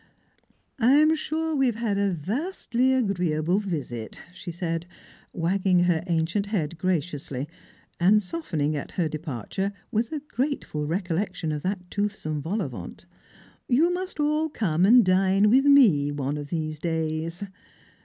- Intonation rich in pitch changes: Yes, wide, 6.7 semitones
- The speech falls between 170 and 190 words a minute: No, average, 155 wpm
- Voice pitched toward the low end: No, medium, 185 Hz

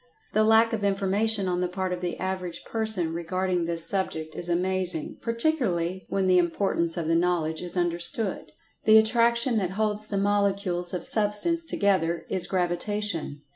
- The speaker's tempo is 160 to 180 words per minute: Yes, average, 165 wpm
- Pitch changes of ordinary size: Yes, average, 3.3 semitones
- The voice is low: No, high, 190 Hz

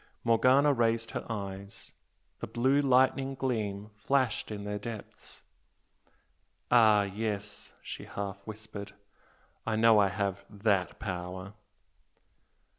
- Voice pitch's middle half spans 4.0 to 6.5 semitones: No, average, 2.8 semitones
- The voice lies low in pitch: Yes, low, 105 Hz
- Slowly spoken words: Yes, slow, 110 wpm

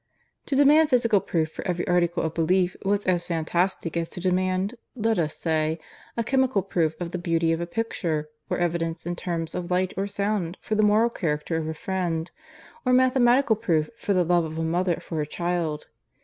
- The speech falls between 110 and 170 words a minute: No, average, 200 wpm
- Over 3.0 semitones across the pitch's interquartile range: Yes, average, 3.7 semitones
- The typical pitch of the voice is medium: Yes, medium, 175 Hz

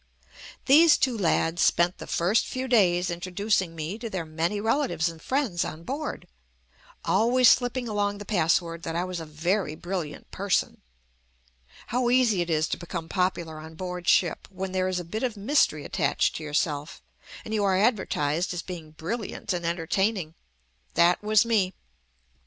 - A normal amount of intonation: Yes, average, 4.5 semitones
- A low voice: No, medium, 185 Hz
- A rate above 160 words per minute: Yes, average, 170 wpm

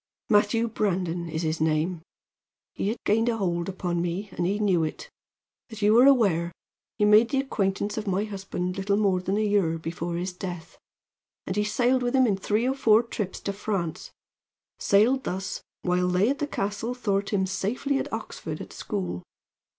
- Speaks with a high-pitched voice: Yes, high, 200 Hz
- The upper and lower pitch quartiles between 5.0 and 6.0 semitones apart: No, average, 3.4 semitones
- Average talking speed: Yes, average, 185 wpm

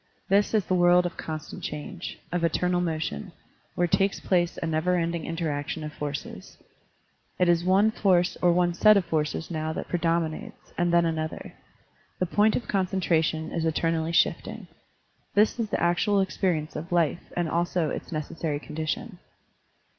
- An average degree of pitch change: No, narrow, 2.3 semitones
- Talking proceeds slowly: No, average, 165 wpm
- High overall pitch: No, medium, 170 Hz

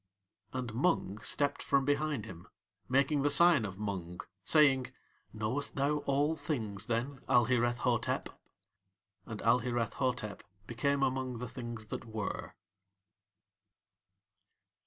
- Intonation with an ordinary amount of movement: Yes, average, 4.0 semitones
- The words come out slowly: Yes, slow, 115 wpm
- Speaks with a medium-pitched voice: No, low, 125 Hz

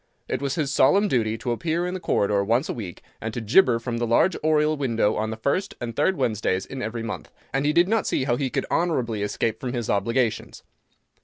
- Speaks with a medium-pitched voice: No, low, 120 Hz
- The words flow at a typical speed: No, fast, 230 wpm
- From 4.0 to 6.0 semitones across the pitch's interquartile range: Yes, average, 5.2 semitones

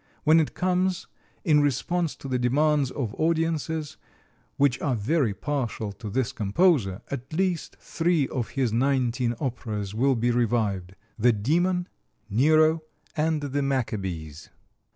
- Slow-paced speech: Yes, slow, 130 wpm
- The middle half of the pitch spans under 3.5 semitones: No, wide, 5.5 semitones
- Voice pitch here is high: No, low, 135 Hz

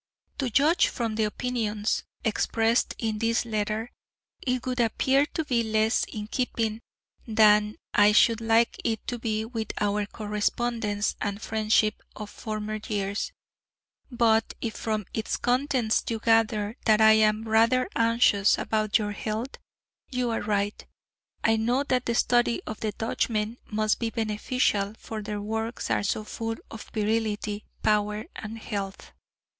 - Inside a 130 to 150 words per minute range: Yes, average, 145 wpm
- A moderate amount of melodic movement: No, narrow, 1.6 semitones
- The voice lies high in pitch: Yes, high, 220 Hz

